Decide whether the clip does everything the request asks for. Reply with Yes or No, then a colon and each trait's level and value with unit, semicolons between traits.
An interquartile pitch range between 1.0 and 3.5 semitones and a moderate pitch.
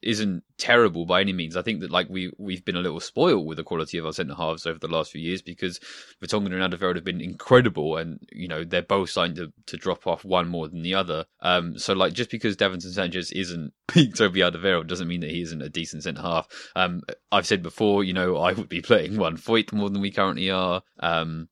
No: narrow, 2.5 semitones; very low, 90 Hz